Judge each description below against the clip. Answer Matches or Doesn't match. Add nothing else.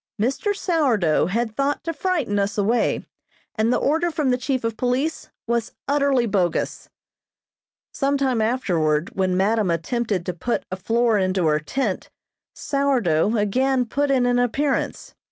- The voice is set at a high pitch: Matches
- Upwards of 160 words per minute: Doesn't match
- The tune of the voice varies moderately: Doesn't match